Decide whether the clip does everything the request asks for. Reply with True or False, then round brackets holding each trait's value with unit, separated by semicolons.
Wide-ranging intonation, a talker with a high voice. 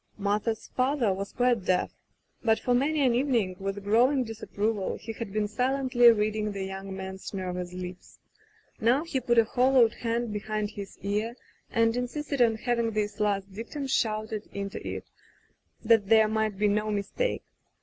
False (3.2 semitones; 220 Hz)